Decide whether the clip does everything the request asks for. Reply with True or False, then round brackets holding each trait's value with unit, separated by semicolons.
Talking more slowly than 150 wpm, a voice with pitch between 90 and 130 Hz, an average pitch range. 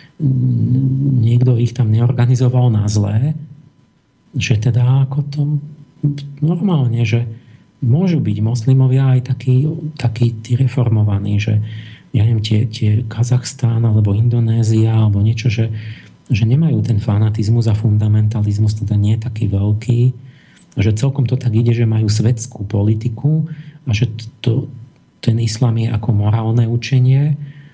True (125 wpm; 120 Hz; 3.1 semitones)